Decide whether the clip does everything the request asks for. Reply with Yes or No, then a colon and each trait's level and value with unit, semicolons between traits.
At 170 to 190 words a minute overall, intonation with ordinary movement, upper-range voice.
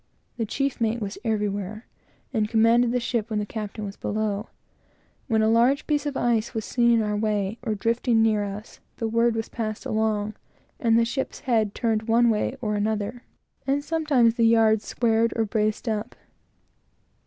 No: average, 175 wpm; narrow, 1.9 semitones; high, 225 Hz